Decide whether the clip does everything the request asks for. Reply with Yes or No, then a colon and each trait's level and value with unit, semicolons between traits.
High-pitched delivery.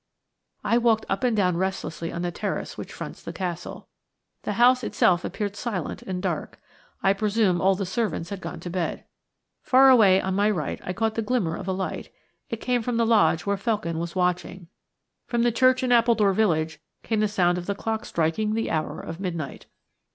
Yes: high, 195 Hz